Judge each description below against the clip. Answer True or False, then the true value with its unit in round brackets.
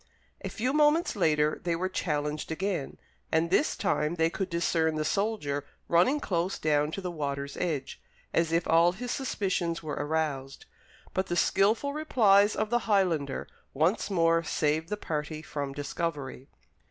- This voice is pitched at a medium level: True (170 Hz)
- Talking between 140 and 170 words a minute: True (155 wpm)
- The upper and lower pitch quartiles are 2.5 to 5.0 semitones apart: True (4.6 semitones)